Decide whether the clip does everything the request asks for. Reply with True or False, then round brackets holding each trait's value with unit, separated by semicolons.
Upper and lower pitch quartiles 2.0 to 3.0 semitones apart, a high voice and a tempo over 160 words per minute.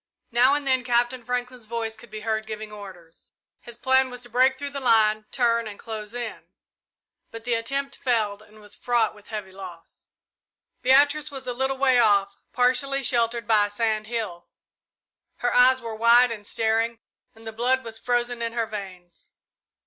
True (2.6 semitones; 230 Hz; 180 wpm)